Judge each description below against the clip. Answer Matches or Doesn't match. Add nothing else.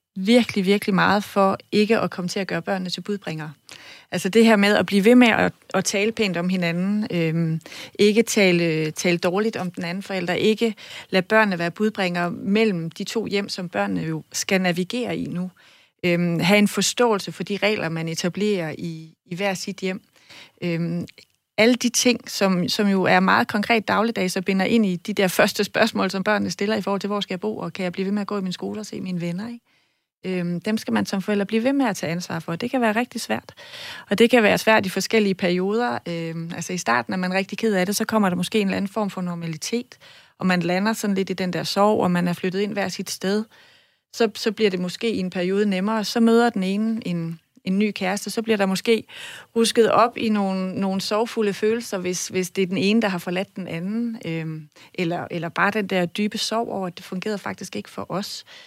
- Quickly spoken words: Matches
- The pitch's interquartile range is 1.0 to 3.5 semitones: Matches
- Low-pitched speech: Doesn't match